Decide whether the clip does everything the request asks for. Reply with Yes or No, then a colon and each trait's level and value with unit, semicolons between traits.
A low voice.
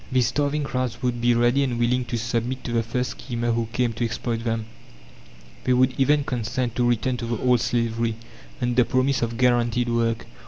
Yes: low, 120 Hz